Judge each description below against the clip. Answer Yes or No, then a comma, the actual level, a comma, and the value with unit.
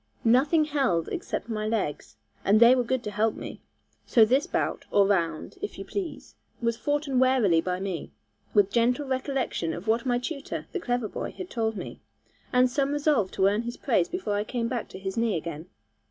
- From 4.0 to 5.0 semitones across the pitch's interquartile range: Yes, average, 4.7 semitones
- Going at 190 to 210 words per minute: Yes, average, 195 wpm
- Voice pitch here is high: Yes, high, 235 Hz